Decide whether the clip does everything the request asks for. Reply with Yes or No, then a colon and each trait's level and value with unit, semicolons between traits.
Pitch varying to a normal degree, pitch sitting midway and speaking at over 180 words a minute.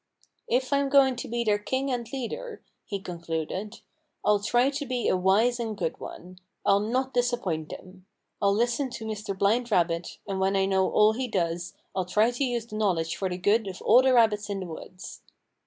No: average, 4.5 semitones; high, 210 Hz; fast, 205 wpm